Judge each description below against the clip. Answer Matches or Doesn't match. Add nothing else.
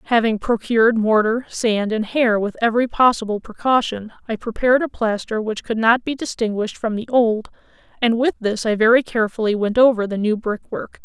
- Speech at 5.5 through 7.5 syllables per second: Matches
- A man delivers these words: Doesn't match